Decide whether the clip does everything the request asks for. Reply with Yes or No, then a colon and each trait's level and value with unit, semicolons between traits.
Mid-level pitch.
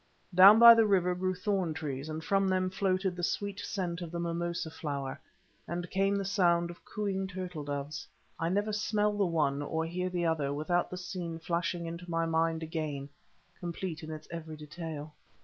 Yes: medium, 170 Hz